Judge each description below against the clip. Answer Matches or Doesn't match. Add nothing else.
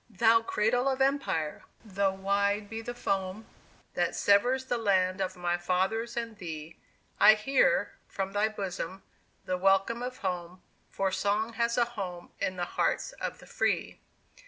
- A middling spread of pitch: Matches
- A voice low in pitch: Doesn't match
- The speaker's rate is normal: Matches